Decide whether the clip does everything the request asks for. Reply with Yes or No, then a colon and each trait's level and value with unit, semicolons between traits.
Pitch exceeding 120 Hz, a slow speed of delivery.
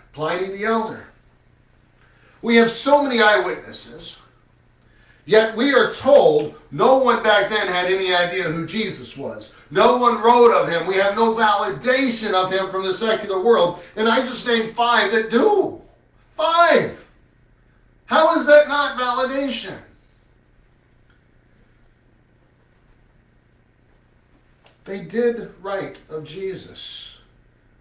Yes: high, 190 Hz; slow, 120 wpm